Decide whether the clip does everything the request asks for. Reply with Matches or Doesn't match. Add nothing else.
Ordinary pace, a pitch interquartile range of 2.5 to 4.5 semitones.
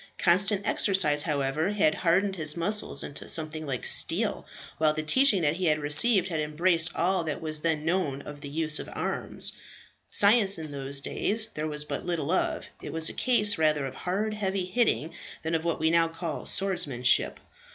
Matches